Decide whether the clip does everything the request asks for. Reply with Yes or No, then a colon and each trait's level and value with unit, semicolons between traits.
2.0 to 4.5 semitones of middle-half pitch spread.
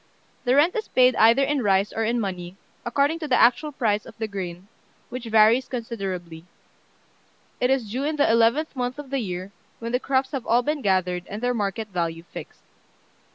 No: average, 5.1 semitones